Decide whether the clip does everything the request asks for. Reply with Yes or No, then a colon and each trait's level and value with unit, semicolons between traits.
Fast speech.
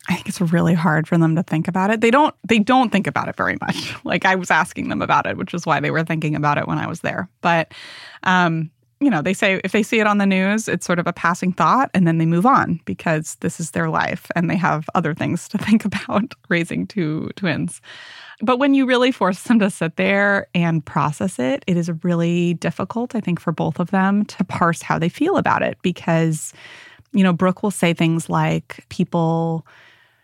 Yes: fast, 230 wpm